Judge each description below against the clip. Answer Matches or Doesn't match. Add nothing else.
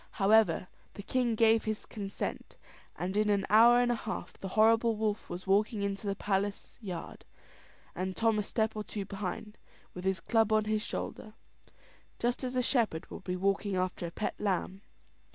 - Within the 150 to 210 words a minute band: Matches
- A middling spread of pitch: Doesn't match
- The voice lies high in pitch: Matches